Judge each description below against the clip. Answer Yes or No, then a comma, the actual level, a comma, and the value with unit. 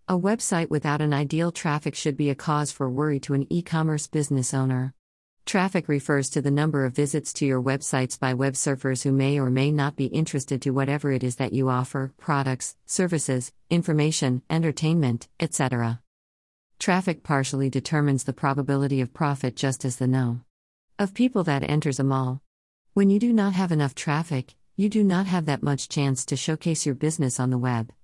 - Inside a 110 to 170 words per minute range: No, average, 185 wpm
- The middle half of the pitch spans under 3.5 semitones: Yes, average, 2.9 semitones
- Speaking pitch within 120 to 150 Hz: Yes, medium, 140 Hz